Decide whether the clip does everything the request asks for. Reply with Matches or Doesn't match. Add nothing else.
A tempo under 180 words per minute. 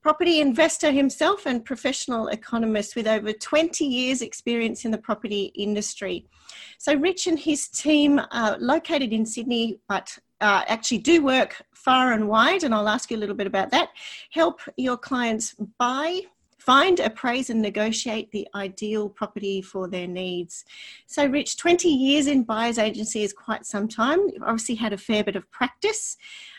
Matches